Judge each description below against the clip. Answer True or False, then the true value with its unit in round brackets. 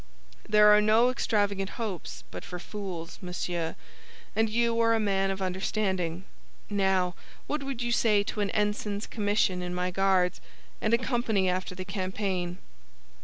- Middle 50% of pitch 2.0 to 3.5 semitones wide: True (2.8 semitones)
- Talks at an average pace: True (155 wpm)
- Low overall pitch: False (200 Hz)